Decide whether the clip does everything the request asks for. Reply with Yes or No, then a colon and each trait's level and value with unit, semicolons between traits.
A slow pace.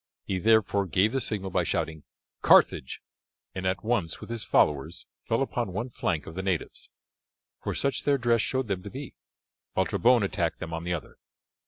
No: average, 185 wpm